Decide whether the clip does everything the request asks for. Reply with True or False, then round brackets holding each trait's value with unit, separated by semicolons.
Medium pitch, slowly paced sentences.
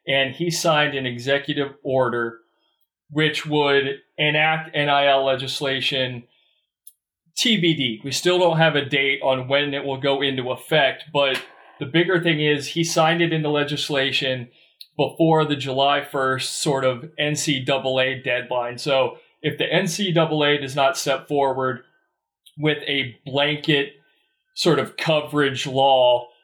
True (145 Hz; 130 wpm)